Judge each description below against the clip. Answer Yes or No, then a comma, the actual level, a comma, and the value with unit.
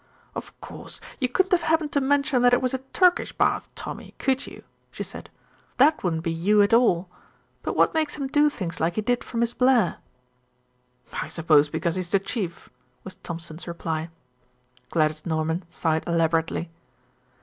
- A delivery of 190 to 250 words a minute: No, average, 170 wpm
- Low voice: No, high, 190 Hz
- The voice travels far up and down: Yes, wide, 8.1 semitones